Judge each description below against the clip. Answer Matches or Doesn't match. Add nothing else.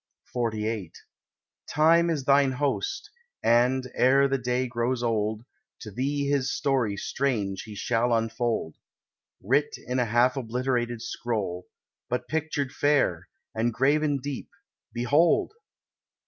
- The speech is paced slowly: Matches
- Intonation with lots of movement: Doesn't match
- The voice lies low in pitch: Matches